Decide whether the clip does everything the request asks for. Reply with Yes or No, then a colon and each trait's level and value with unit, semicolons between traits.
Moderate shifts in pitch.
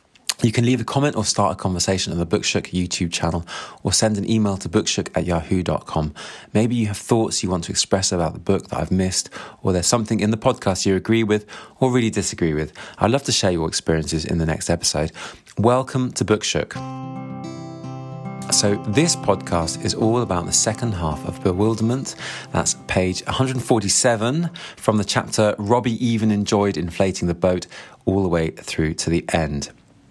Yes: average, 4.8 semitones